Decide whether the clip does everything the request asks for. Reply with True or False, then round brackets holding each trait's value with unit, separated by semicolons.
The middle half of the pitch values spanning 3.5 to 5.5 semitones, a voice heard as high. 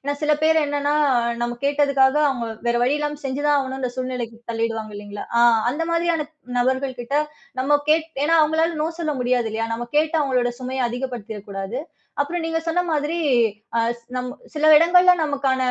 True (3.9 semitones; 270 Hz)